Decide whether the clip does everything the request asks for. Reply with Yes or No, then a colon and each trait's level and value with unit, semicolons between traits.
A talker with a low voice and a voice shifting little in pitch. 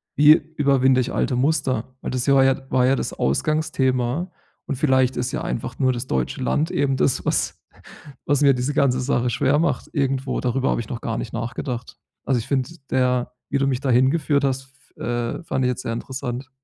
Yes: low, 130 Hz; narrow, 2.0 semitones